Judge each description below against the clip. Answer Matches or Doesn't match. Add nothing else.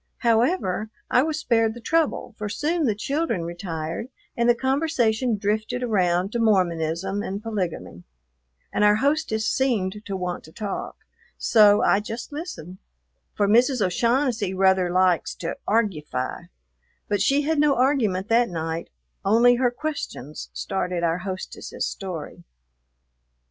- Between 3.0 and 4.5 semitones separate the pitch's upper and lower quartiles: Doesn't match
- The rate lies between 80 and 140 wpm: Matches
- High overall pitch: Matches